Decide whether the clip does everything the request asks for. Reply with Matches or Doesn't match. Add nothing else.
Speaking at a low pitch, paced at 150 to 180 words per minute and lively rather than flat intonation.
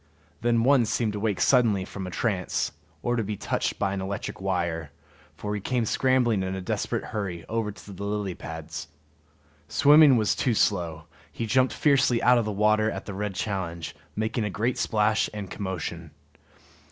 Doesn't match